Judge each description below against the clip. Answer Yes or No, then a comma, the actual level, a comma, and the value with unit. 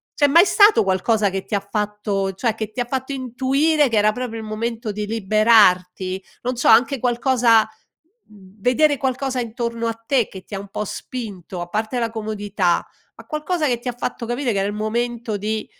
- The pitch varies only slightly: No, average, 3.3 semitones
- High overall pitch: Yes, high, 225 Hz